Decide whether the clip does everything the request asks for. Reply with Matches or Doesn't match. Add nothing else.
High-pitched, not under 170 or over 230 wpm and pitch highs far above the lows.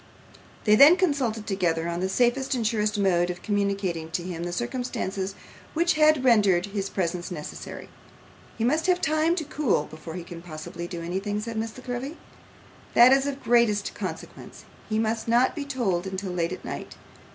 Matches